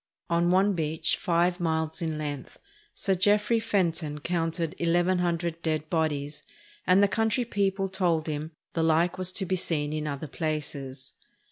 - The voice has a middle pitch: Yes, medium, 170 Hz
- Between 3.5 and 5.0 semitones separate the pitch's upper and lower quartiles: No, average, 3.1 semitones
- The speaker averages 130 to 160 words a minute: Yes, average, 155 wpm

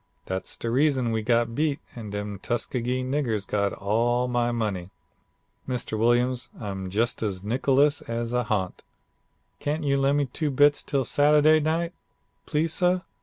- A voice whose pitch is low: Yes, low, 120 Hz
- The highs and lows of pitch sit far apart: No, average, 4.7 semitones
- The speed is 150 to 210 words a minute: Yes, average, 155 wpm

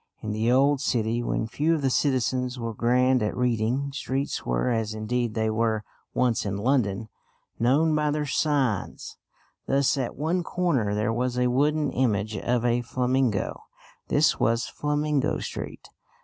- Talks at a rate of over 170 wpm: No, average, 155 wpm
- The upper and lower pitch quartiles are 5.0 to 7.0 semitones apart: No, average, 3.8 semitones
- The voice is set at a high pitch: No, low, 125 Hz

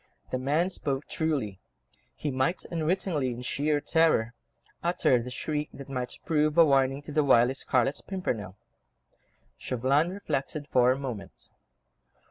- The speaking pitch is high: No, medium, 140 Hz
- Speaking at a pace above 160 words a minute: No, slow, 135 wpm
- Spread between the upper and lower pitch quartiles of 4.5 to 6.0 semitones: No, average, 3.6 semitones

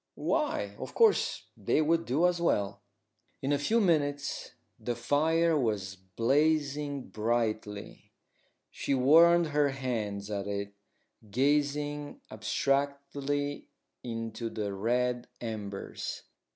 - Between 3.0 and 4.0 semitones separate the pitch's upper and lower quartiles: No, average, 5.3 semitones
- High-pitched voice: No, low, 135 Hz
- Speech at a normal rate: No, slow, 105 wpm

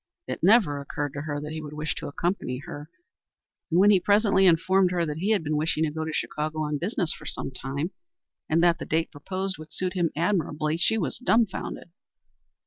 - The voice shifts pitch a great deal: No, average, 3.7 semitones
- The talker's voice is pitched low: No, medium, 160 Hz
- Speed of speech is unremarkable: No, fast, 210 wpm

